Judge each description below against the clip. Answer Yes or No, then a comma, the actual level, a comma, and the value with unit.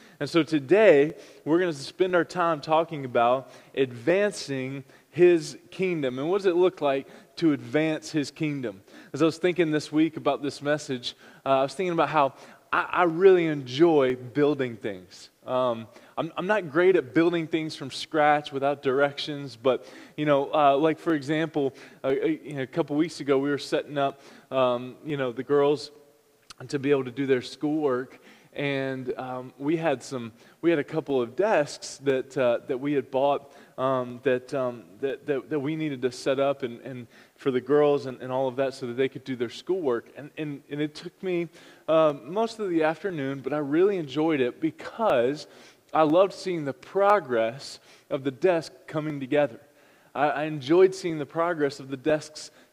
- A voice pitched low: No, medium, 145 Hz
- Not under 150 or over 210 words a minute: Yes, average, 190 wpm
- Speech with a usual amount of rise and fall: Yes, average, 3.2 semitones